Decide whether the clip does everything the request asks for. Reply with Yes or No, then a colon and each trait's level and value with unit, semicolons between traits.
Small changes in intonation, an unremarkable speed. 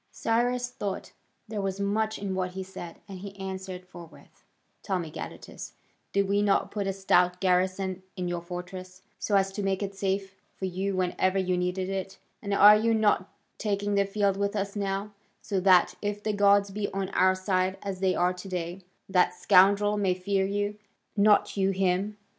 Yes: narrow, 1.5 semitones; average, 190 wpm